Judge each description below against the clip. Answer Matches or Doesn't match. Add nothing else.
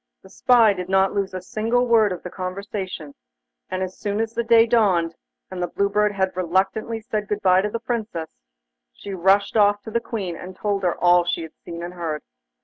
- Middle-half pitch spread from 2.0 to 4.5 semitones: Matches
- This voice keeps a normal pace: Doesn't match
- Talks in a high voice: Matches